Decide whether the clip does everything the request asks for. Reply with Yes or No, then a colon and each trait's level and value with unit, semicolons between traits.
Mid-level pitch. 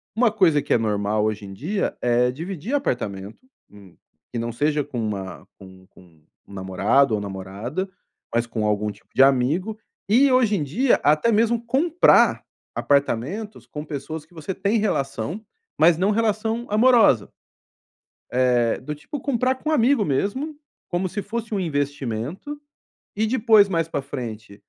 Yes: medium, 150 Hz